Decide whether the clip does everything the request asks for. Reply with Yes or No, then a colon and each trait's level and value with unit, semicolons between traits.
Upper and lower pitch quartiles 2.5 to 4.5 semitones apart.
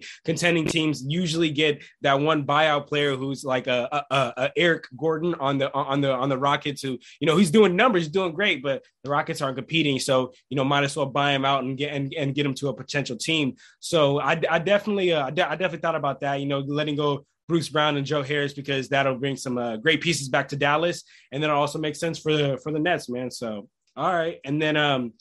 Yes: average, 2.8 semitones